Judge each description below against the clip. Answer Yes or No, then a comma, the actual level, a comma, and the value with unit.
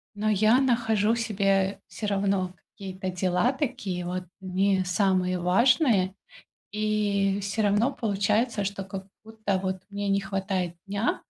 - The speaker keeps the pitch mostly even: Yes, narrow, 2.3 semitones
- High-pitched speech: Yes, high, 200 Hz